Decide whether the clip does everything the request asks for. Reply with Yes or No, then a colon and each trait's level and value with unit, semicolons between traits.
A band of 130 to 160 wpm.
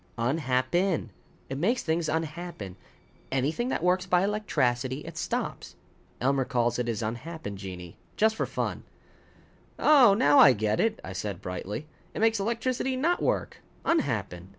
Yes: average, 150 wpm